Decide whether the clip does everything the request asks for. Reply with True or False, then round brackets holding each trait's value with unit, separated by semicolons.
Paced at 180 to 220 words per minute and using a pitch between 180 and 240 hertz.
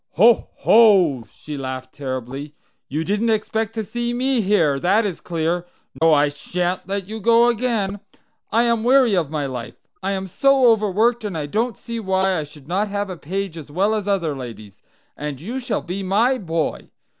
True (190 wpm; 190 Hz)